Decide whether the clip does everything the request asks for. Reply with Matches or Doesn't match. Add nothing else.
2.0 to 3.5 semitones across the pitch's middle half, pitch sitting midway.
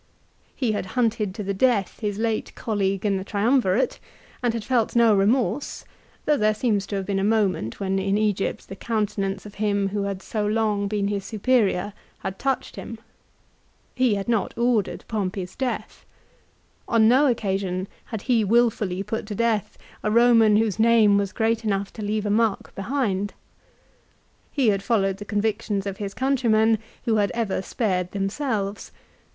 Doesn't match